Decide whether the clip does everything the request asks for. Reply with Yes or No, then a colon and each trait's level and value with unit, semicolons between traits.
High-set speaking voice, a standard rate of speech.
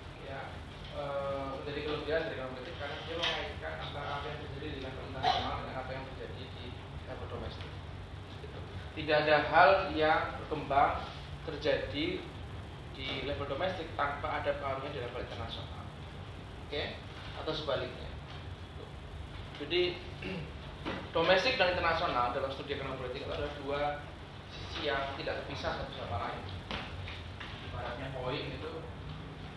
No: low, 130 Hz; average, 130 wpm